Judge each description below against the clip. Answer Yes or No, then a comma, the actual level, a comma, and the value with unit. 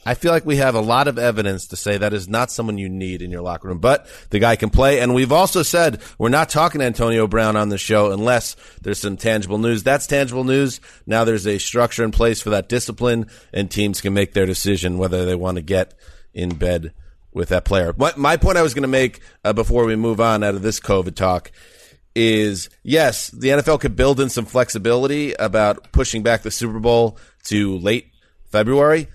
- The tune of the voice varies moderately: Yes, average, 3.7 semitones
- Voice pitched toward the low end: Yes, low, 110 Hz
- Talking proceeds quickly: Yes, fast, 220 wpm